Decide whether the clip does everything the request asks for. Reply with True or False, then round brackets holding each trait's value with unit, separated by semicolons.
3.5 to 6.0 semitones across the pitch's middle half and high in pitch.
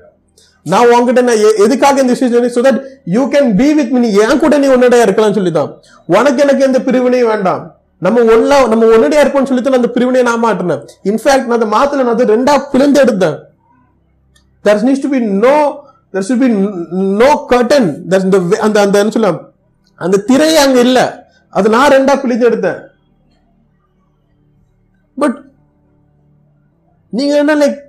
True (4.7 semitones; 245 Hz)